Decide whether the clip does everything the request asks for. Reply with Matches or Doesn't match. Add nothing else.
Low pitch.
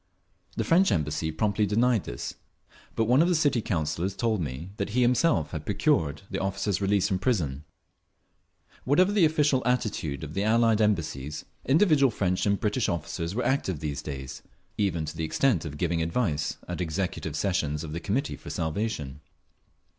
Matches